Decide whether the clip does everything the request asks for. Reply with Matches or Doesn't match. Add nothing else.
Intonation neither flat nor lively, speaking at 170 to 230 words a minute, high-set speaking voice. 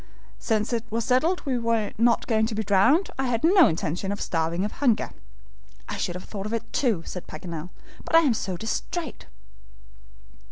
Matches